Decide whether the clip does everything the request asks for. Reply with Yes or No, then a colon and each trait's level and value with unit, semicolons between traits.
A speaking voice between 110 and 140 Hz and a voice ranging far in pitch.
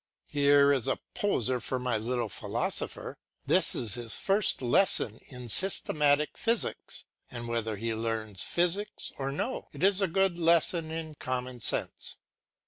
Yes: low, 135 Hz; wide, 6.4 semitones